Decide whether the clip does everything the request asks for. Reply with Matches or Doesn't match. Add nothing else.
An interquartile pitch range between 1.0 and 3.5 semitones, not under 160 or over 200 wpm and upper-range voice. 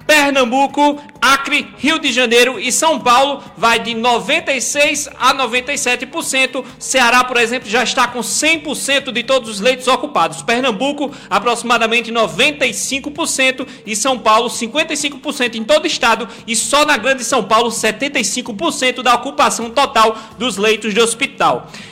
Doesn't match